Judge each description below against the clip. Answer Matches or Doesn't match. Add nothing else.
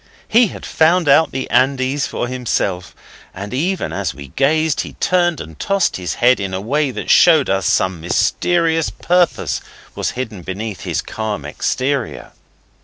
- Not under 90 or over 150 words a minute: Doesn't match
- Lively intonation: Matches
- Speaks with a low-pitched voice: Matches